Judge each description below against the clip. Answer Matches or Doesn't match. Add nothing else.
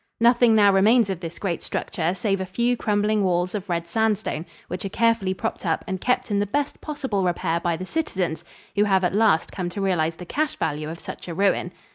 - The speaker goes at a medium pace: Doesn't match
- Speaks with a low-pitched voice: Doesn't match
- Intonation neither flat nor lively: Matches